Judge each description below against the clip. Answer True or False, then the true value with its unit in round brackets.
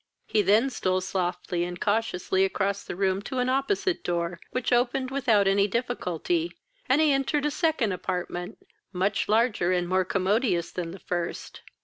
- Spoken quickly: False (160 wpm)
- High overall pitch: True (200 Hz)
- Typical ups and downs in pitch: False (5.8 semitones)